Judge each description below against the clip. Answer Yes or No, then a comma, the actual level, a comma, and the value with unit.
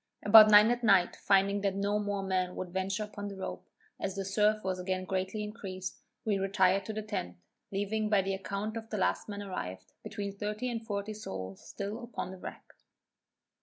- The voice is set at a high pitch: Yes, high, 200 Hz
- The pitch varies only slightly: Yes, narrow, 1.9 semitones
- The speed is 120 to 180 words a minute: No, average, 195 wpm